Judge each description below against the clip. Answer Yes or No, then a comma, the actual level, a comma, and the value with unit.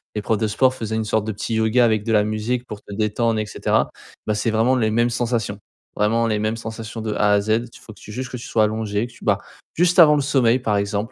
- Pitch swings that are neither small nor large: No, narrow, 1.9 semitones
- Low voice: Yes, low, 110 Hz